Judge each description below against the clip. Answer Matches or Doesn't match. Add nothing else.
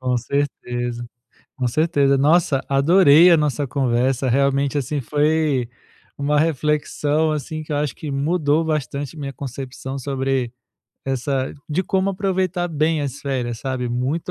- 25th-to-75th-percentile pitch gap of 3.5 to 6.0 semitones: Doesn't match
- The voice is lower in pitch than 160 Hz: Matches